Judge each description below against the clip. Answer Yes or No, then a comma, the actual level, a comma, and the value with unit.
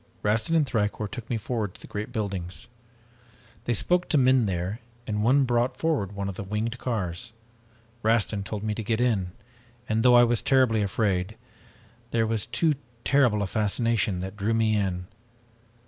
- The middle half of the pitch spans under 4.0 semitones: Yes, average, 3.1 semitones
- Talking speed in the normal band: Yes, average, 175 wpm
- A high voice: No, low, 110 Hz